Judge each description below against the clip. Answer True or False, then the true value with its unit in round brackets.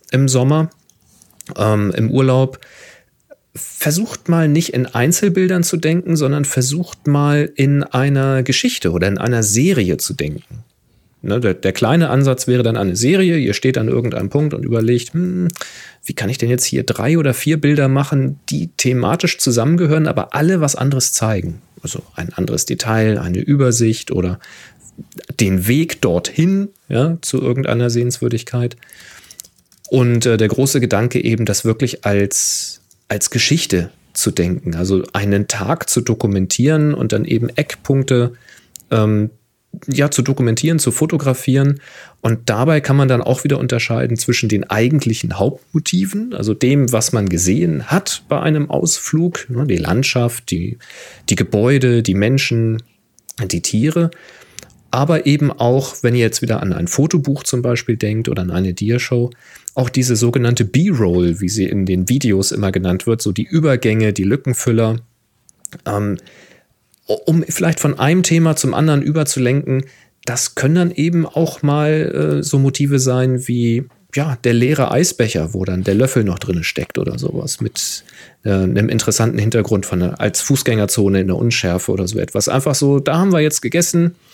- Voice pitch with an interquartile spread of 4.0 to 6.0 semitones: True (4.7 semitones)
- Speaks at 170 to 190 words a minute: False (160 wpm)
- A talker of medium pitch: False (125 Hz)